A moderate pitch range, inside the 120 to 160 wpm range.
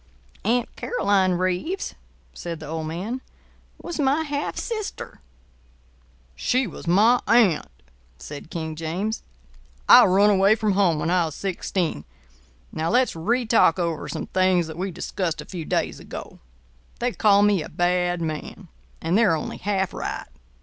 Yes: average, 4.7 semitones; average, 150 wpm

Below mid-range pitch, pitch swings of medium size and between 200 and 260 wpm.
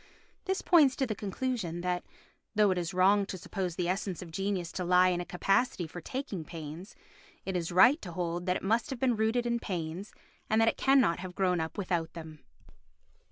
No: medium, 185 Hz; average, 4.0 semitones; fast, 205 wpm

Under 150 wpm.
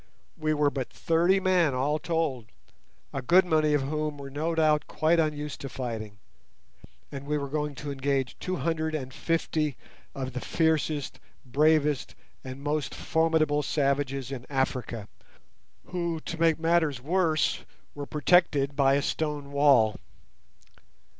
Yes: average, 140 wpm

